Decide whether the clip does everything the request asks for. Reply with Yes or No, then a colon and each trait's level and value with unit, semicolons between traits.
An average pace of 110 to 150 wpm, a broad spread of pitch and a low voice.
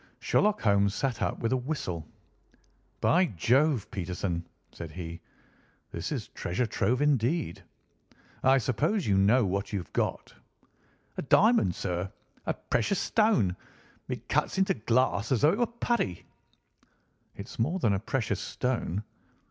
Yes: average, 140 wpm; wide, 7.3 semitones; low, 115 Hz